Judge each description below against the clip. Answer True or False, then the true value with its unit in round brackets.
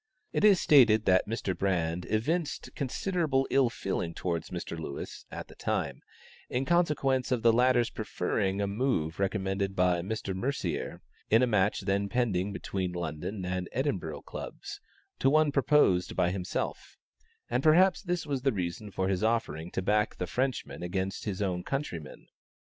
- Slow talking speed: False (160 wpm)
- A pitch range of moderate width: False (6.4 semitones)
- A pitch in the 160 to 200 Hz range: False (100 Hz)